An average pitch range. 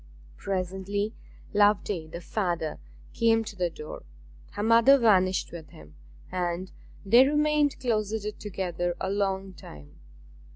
Yes: average, 3.8 semitones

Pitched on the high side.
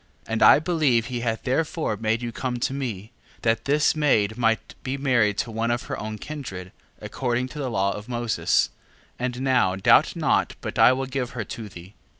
No: low, 120 Hz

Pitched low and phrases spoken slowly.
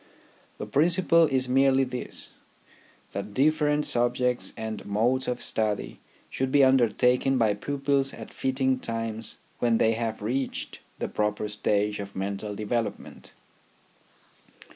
Yes: low, 125 Hz; slow, 120 wpm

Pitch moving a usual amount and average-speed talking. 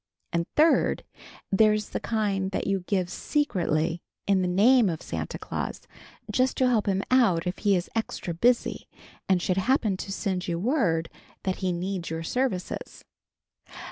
Yes: average, 4.1 semitones; average, 160 wpm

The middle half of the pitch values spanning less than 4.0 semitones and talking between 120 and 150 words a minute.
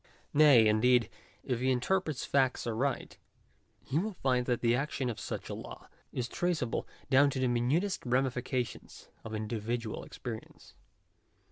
Yes: average, 2.7 semitones; average, 140 wpm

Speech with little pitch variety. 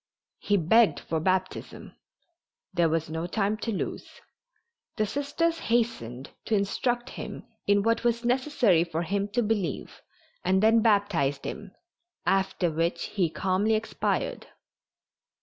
No: average, 4.8 semitones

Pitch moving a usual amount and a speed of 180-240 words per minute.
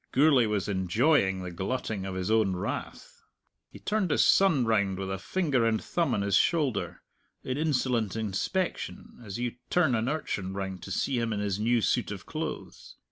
No: wide, 5.7 semitones; average, 185 wpm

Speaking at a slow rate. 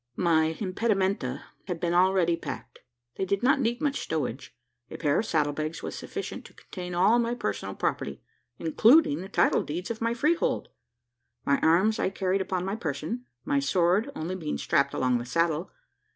No: average, 175 wpm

